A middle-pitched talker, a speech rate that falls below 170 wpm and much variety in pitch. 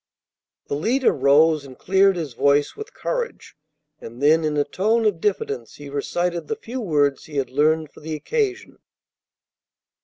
Yes: medium, 155 Hz; average, 160 wpm; wide, 6.2 semitones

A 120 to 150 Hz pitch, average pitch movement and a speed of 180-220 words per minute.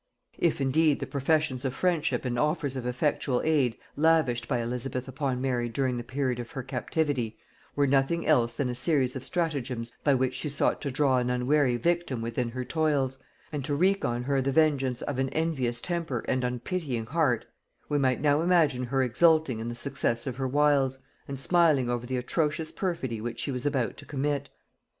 Yes: low, 135 Hz; average, 3.4 semitones; average, 190 wpm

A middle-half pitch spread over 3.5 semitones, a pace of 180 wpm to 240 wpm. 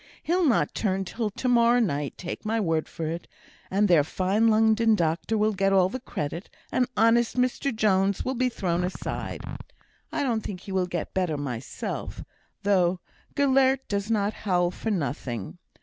No: average, 4.4 semitones; average, 170 wpm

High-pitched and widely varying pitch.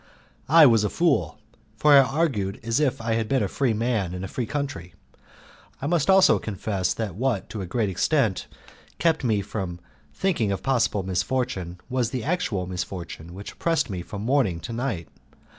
No: low, 115 Hz; wide, 5.9 semitones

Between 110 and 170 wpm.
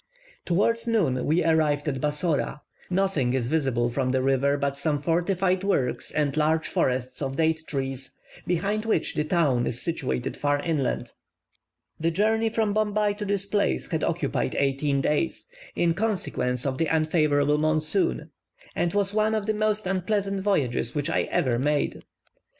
Yes: average, 155 wpm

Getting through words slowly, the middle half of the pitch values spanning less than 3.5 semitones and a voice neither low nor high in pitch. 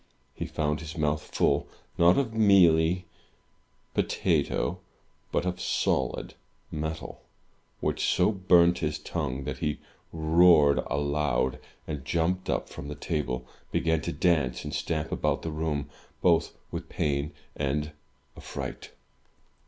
No: slow, 125 wpm; average, 2.9 semitones; very low, 80 Hz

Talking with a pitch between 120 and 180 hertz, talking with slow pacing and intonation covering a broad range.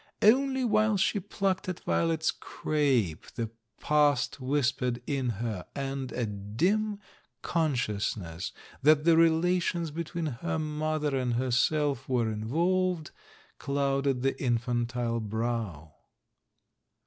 Yes: medium, 140 Hz; slow, 110 wpm; wide, 5.8 semitones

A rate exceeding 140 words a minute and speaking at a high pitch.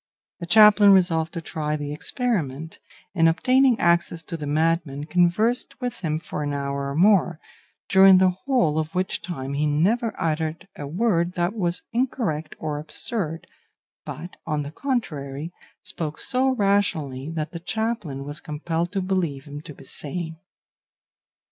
No: average, 155 wpm; medium, 165 Hz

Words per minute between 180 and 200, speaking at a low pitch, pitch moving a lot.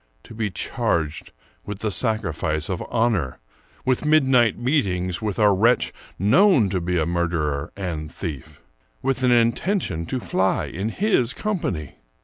No: average, 140 wpm; low, 100 Hz; wide, 6.4 semitones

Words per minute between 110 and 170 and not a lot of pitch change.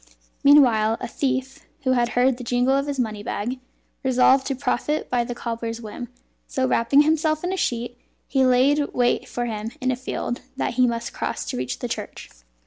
No: average, 195 wpm; narrow, 2.3 semitones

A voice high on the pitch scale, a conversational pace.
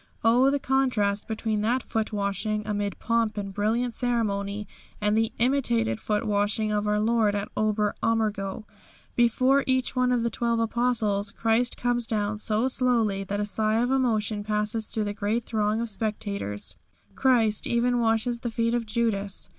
Yes: high, 220 Hz; average, 165 wpm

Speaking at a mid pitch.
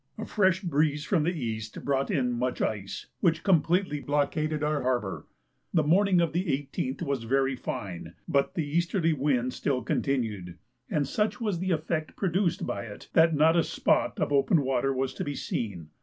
Yes: medium, 145 Hz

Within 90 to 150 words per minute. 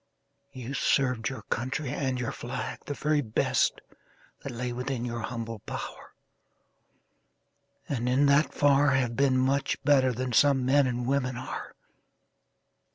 Yes: average, 140 wpm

